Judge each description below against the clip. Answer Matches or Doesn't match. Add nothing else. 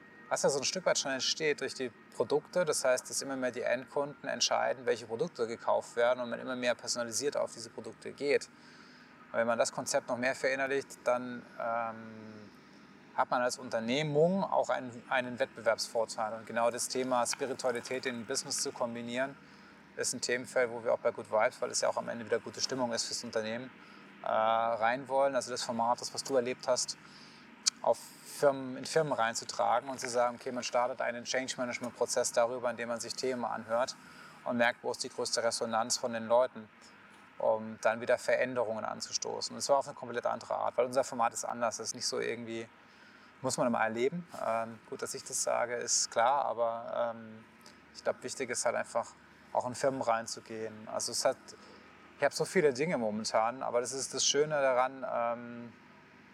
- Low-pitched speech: Matches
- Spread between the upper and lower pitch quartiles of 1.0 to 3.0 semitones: Matches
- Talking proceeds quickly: Matches